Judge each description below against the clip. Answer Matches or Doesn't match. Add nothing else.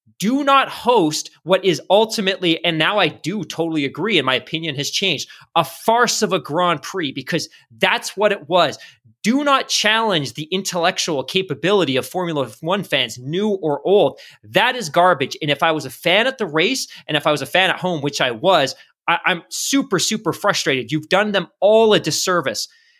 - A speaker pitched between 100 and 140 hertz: Doesn't match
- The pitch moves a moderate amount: Matches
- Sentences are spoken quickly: Doesn't match